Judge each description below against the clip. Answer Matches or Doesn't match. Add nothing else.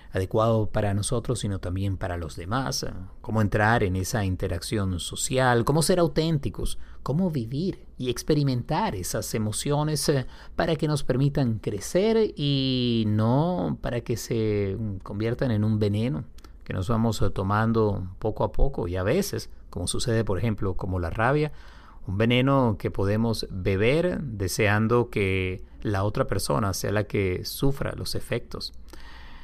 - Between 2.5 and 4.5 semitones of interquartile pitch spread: Doesn't match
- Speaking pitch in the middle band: Doesn't match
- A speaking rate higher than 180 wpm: Doesn't match